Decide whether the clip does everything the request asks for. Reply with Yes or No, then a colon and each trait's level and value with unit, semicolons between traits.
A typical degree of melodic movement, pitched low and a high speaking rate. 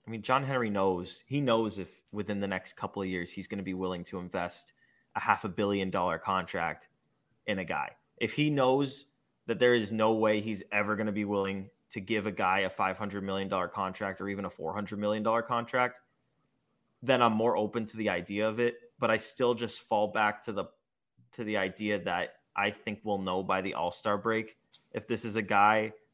Yes: average, 3.2 semitones; low, 105 Hz; fast, 215 wpm